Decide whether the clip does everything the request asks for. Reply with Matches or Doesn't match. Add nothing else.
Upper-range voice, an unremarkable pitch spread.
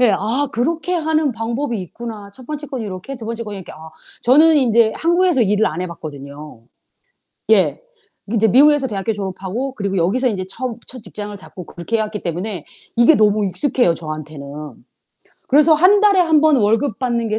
Doesn't match